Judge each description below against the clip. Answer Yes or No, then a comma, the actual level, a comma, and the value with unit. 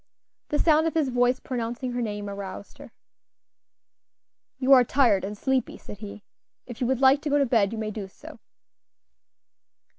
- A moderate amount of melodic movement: Yes, average, 4.2 semitones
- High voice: Yes, high, 245 Hz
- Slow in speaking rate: No, average, 175 wpm